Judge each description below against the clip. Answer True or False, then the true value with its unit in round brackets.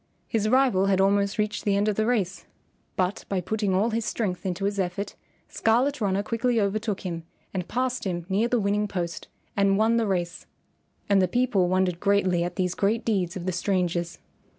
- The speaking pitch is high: True (200 Hz)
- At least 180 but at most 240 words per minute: True (195 wpm)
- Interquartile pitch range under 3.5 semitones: True (2.9 semitones)